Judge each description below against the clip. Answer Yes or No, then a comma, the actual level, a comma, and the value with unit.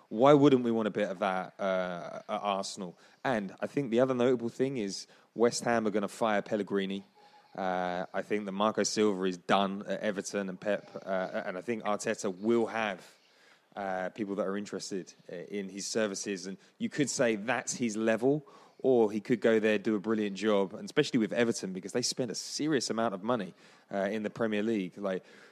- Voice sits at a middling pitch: No, low, 105 Hz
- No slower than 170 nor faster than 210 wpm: Yes, fast, 205 wpm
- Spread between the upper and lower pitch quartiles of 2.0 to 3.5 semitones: Yes, average, 2.9 semitones